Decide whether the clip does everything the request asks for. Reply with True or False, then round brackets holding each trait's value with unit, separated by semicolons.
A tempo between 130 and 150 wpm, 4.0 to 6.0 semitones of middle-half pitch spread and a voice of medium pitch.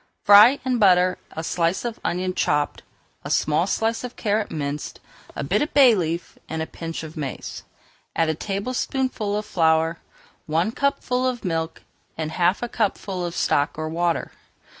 False (165 wpm; 5.5 semitones; 180 Hz)